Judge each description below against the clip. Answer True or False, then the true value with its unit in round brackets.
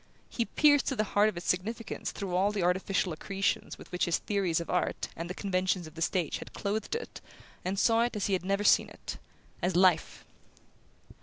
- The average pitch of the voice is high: True (195 Hz)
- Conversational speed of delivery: False (210 wpm)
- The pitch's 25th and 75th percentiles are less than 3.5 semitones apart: True (2.8 semitones)